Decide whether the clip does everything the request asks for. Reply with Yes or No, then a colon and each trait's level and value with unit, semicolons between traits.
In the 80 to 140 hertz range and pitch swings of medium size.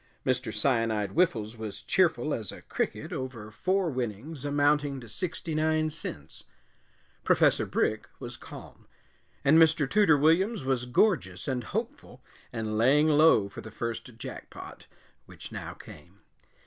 No: low, 135 Hz; wide, 5.9 semitones